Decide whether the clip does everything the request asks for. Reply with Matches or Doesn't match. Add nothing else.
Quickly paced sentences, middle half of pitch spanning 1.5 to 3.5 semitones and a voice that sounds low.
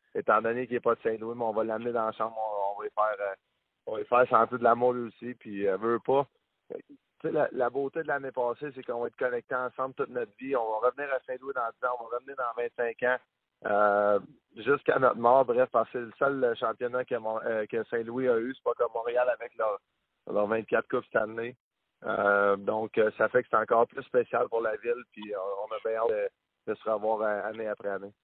Doesn't match